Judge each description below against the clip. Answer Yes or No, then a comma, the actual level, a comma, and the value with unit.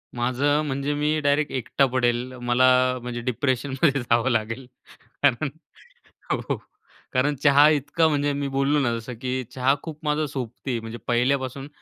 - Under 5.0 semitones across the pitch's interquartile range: Yes, average, 2.7 semitones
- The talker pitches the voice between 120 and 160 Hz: Yes, low, 135 Hz